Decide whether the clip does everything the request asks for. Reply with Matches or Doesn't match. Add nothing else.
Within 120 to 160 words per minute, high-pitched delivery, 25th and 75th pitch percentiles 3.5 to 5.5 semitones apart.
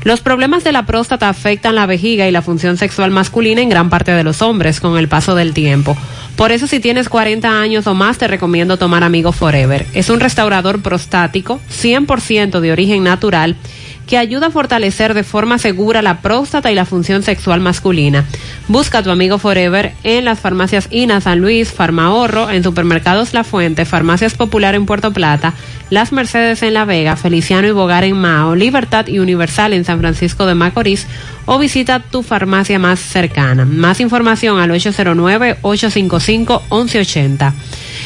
Doesn't match